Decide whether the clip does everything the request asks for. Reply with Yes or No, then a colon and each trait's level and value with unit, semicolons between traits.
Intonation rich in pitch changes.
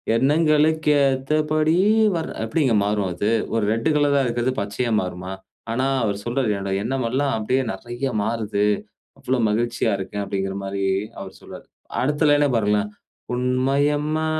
Yes: wide, 5.8 semitones